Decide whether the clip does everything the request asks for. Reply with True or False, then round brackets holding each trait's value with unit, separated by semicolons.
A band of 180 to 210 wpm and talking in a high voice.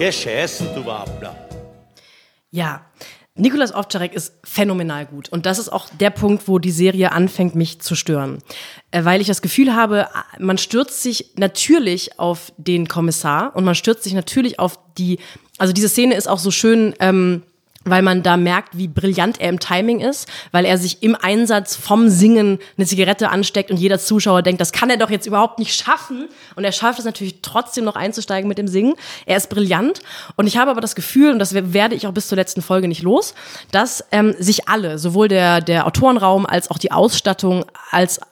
True (190 wpm; 195 Hz)